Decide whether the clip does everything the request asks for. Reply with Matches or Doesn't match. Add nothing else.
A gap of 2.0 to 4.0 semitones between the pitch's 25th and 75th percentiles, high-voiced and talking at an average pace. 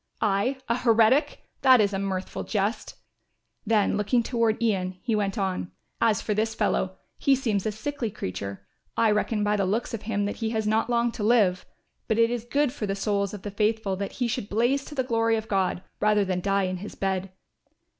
Doesn't match